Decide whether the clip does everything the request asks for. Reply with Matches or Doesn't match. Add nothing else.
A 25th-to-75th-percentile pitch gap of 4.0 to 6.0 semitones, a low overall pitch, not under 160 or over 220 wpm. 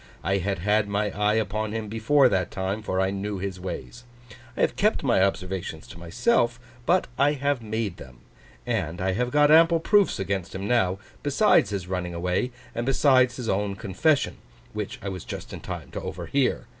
Matches